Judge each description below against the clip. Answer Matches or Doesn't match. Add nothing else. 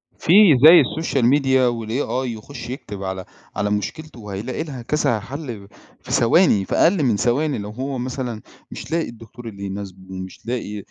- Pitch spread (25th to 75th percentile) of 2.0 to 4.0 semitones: Doesn't match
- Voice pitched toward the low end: Matches